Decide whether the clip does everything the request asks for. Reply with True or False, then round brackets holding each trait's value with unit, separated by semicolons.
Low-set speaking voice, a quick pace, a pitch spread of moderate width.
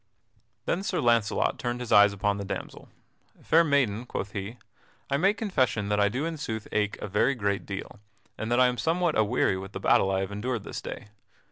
True (110 Hz; 210 wpm; 4.8 semitones)